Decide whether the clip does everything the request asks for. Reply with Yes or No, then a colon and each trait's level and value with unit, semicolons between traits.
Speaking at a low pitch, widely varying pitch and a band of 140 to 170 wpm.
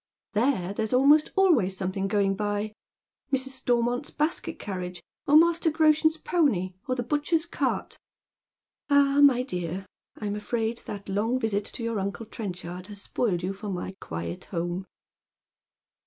No: high, 220 Hz; wide, 6.3 semitones; average, 155 wpm